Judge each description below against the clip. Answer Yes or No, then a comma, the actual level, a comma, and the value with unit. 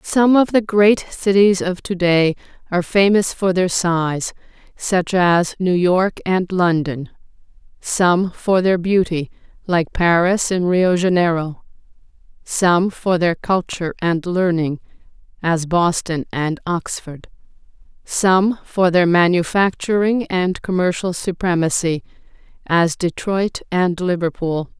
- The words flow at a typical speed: No, slow, 115 wpm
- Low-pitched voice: No, medium, 180 Hz